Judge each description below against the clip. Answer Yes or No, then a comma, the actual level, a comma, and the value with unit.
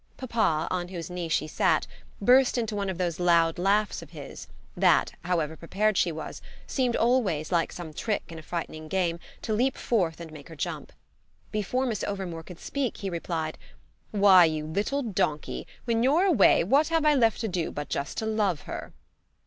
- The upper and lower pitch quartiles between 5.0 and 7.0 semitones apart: Yes, wide, 5.4 semitones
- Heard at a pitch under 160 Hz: No, medium, 185 Hz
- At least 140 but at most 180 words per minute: No, average, 190 wpm